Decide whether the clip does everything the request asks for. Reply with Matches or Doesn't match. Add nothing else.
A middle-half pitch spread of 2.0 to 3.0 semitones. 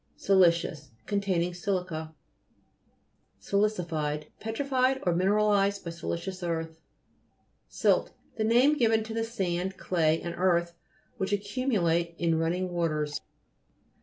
Doesn't match